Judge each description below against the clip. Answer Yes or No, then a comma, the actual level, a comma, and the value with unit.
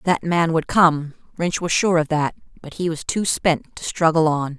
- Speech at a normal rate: No, fast, 220 wpm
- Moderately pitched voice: Yes, medium, 160 Hz